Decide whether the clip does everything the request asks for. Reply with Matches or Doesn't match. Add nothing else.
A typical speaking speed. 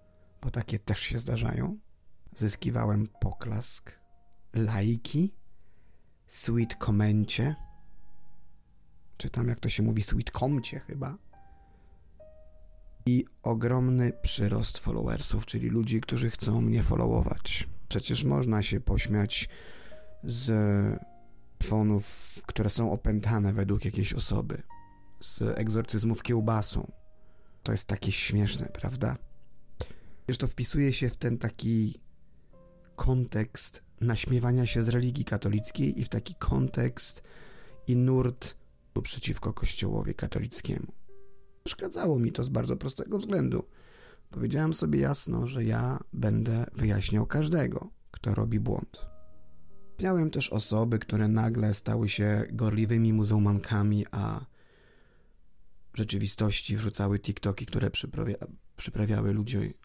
Doesn't match